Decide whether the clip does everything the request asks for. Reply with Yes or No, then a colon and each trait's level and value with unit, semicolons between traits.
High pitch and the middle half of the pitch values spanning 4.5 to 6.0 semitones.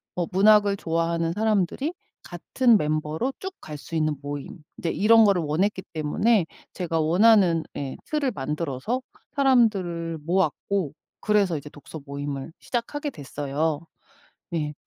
No: medium, 170 Hz; wide, 5.6 semitones